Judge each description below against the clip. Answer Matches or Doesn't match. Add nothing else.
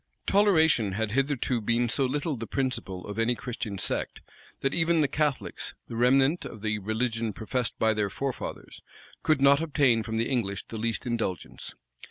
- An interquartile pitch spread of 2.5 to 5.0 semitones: Matches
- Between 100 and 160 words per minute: Doesn't match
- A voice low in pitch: Matches